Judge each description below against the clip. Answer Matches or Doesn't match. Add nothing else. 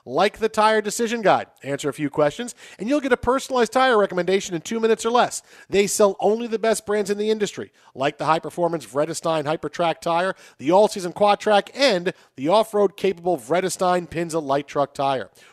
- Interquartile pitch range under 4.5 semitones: Doesn't match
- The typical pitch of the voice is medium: Doesn't match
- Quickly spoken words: Doesn't match